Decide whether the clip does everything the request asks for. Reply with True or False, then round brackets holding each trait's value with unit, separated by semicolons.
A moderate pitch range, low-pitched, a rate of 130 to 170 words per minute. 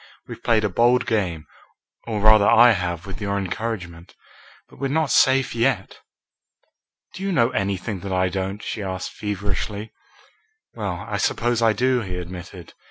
True (3.8 semitones; 105 Hz; 160 wpm)